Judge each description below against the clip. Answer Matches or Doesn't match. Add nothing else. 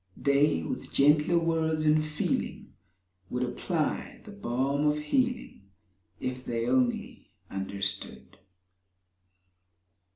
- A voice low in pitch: Doesn't match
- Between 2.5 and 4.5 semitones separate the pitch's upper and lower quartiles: Matches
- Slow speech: Matches